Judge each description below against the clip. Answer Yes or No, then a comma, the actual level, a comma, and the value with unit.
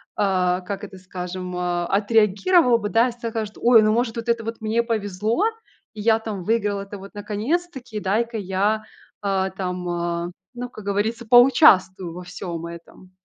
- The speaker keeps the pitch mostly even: No, average, 3.7 semitones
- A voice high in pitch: Yes, high, 205 Hz